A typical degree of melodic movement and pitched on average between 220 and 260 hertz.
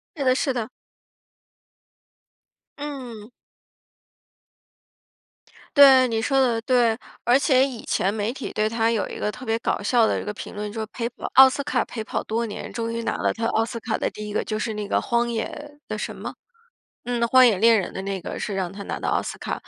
Yes: average, 3.0 semitones; high, 230 Hz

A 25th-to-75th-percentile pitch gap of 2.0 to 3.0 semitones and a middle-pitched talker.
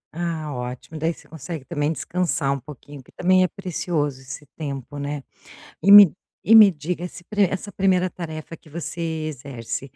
No: average, 3.9 semitones; medium, 160 Hz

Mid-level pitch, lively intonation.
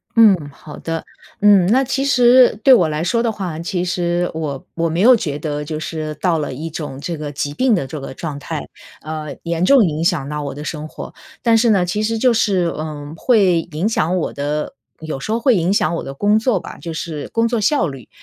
Yes: medium, 170 Hz; wide, 5.9 semitones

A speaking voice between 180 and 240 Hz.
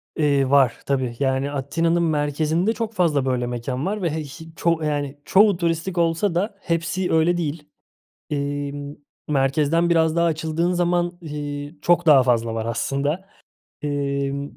No: medium, 150 Hz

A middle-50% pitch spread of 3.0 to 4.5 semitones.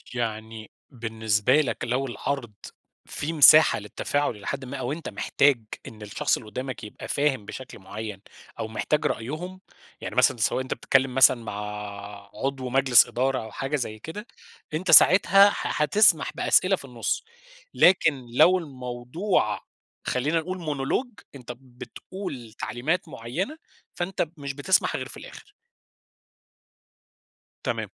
No: average, 5.0 semitones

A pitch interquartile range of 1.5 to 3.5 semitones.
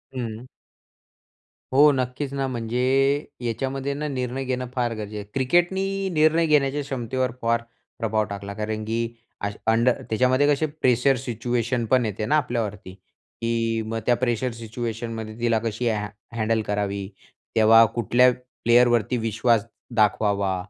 Yes: average, 2.7 semitones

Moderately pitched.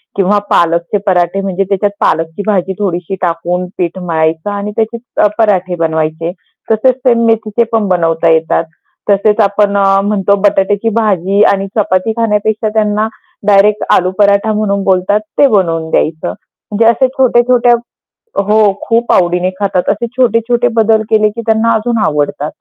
No: high, 200 Hz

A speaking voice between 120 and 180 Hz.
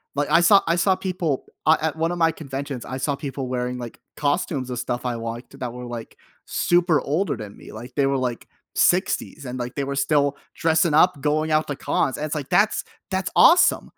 Yes: medium, 140 Hz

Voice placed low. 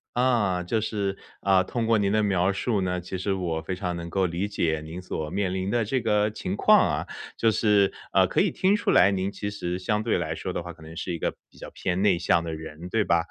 Yes: very low, 95 Hz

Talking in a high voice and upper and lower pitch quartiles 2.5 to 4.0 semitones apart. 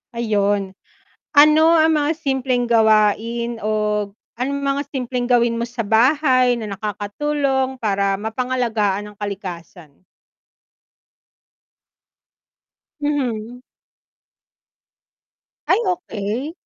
No: high, 235 Hz; average, 4.5 semitones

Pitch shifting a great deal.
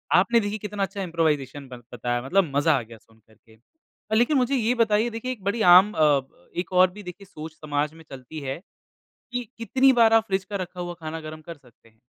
Yes: wide, 6.8 semitones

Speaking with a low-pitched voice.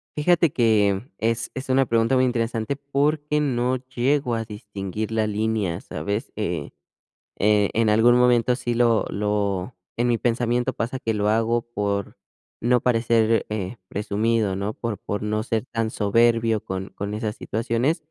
Yes: low, 115 Hz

